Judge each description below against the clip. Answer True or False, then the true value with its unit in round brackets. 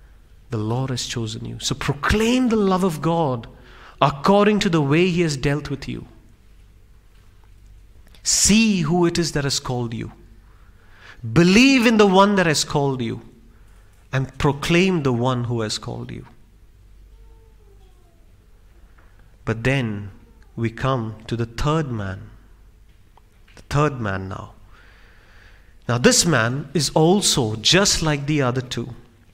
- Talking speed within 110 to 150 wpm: True (135 wpm)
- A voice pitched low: True (115 Hz)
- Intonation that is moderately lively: False (6.6 semitones)